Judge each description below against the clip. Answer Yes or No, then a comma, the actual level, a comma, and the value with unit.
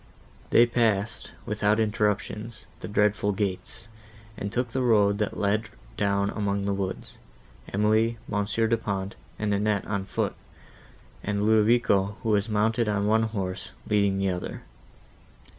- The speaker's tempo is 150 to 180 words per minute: No, average, 140 wpm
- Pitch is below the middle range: Yes, low, 105 Hz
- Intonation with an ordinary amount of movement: No, narrow, 1.7 semitones